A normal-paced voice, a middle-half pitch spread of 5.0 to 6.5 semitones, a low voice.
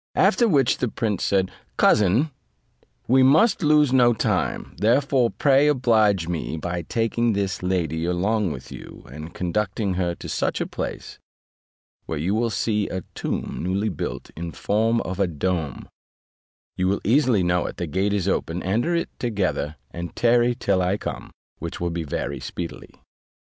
Yes: average, 165 wpm; average, 5.3 semitones; low, 100 Hz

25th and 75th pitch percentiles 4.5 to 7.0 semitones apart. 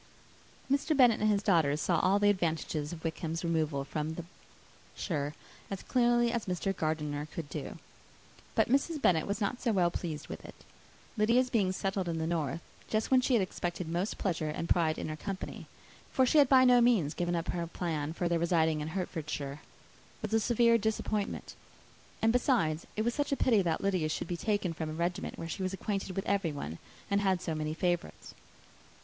Yes: average, 5.1 semitones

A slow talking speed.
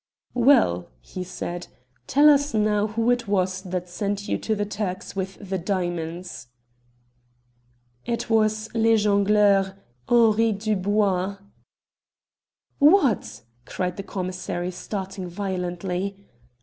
Yes: slow, 110 wpm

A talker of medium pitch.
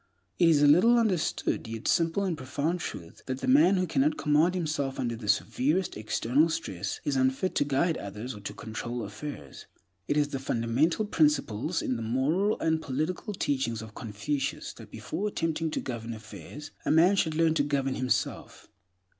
Yes: medium, 145 Hz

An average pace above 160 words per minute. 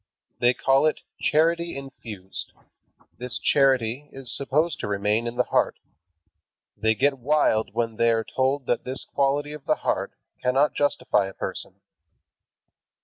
No: average, 145 wpm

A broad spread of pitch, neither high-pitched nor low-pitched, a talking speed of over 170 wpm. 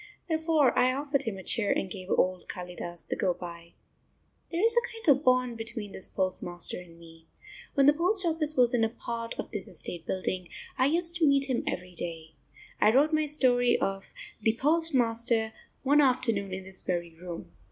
No: wide, 7.6 semitones; high, 230 Hz; average, 190 wpm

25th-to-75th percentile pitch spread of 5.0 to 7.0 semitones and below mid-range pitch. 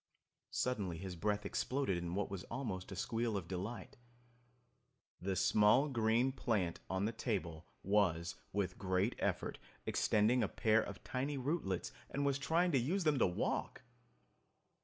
Yes: wide, 5.4 semitones; low, 105 Hz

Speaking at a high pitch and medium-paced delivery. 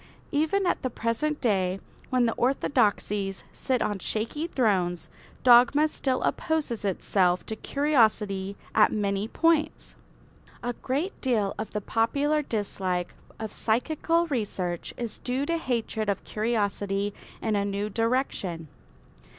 No: high, 225 Hz; slow, 125 wpm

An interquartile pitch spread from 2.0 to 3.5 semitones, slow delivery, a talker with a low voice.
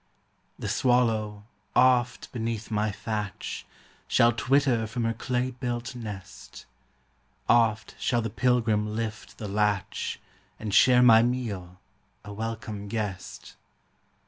Yes: narrow, 2.5 semitones; slow, 115 wpm; low, 115 Hz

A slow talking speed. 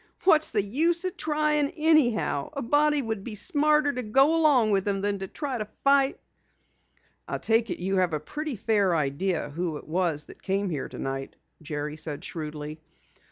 No: average, 175 wpm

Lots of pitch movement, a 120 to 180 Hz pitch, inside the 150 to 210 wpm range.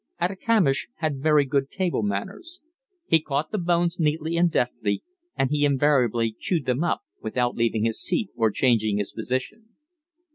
Yes: wide, 6.2 semitones; medium, 140 Hz; average, 155 wpm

